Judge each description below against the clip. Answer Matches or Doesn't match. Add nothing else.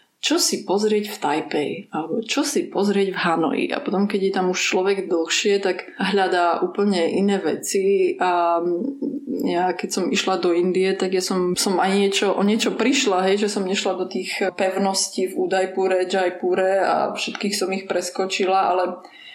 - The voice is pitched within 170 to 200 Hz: Matches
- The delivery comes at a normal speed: Doesn't match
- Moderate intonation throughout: Doesn't match